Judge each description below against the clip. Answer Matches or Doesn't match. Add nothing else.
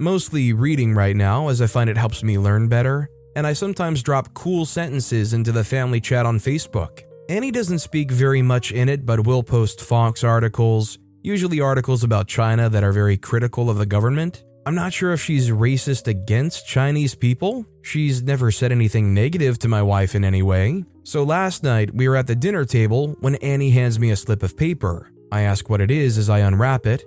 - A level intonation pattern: Doesn't match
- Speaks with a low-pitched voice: Matches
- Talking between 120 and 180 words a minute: Doesn't match